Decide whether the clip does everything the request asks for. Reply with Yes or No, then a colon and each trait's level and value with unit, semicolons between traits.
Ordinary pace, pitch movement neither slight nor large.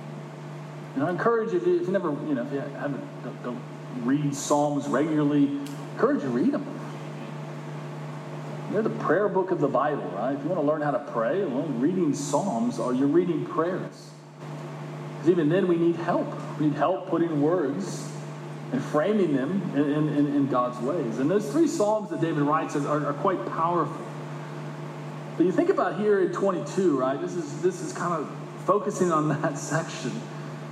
Yes: average, 185 wpm; average, 3.9 semitones